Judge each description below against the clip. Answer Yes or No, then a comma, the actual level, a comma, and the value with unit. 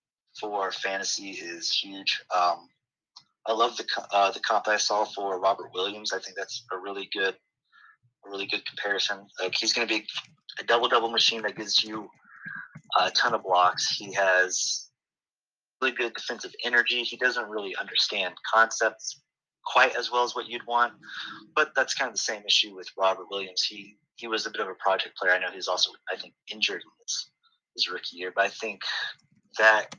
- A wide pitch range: No, average, 3.2 semitones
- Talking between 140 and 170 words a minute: No, average, 190 wpm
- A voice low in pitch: Yes, low, 115 Hz